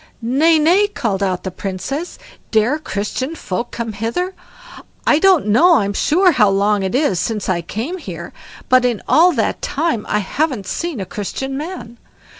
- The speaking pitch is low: No, high, 240 Hz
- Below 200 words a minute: Yes, average, 170 wpm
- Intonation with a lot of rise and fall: Yes, wide, 7.7 semitones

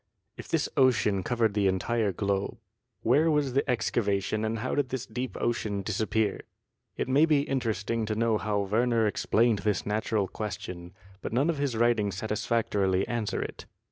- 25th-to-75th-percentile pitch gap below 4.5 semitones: Yes, average, 3.1 semitones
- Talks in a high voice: No, low, 110 Hz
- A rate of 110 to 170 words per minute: Yes, average, 165 wpm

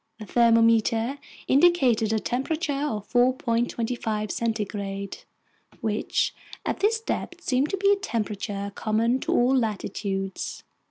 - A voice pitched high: Yes, high, 230 Hz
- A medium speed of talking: No, slow, 120 wpm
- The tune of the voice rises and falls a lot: No, average, 3.9 semitones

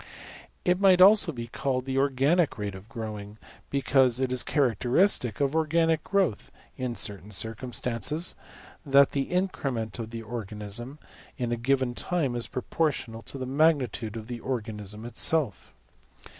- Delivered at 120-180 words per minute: Yes, average, 145 wpm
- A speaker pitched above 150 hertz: No, low, 125 Hz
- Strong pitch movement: No, average, 4.3 semitones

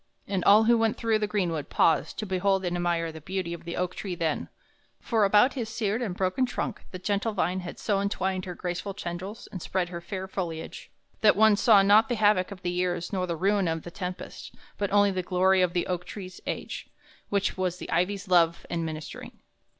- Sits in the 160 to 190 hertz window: Yes, medium, 185 Hz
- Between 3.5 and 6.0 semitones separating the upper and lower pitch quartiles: No, narrow, 2.6 semitones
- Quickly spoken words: Yes, fast, 215 wpm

